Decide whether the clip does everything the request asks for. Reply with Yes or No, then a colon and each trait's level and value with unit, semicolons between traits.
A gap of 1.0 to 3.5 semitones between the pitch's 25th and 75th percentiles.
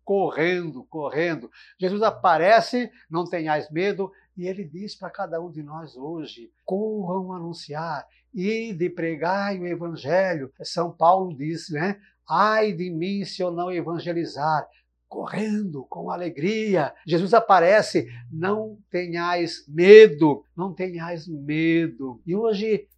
Yes: average, 3.2 semitones